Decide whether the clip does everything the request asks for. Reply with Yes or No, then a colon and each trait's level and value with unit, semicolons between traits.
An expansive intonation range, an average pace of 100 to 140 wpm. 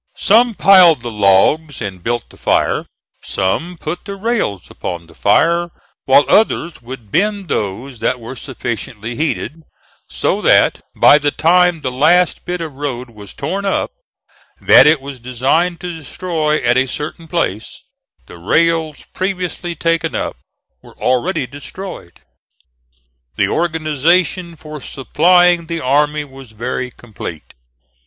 Yes: wide, 6.0 semitones; slow, 135 wpm